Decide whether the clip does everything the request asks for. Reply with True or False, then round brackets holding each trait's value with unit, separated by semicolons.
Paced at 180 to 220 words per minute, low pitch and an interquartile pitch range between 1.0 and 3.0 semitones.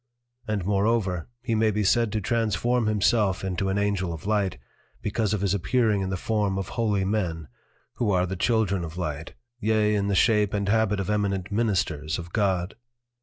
True (185 wpm; 100 Hz; 2.5 semitones)